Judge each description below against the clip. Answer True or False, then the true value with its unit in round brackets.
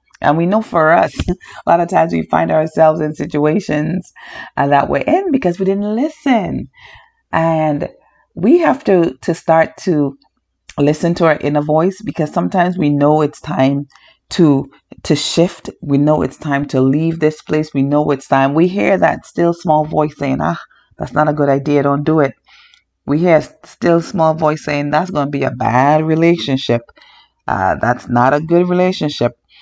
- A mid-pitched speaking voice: True (155 Hz)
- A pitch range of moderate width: True (3.1 semitones)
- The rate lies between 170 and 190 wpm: True (185 wpm)